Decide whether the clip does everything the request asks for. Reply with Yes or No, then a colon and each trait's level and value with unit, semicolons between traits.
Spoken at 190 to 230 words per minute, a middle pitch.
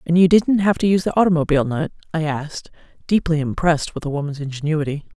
Yes: average, 195 wpm; medium, 160 Hz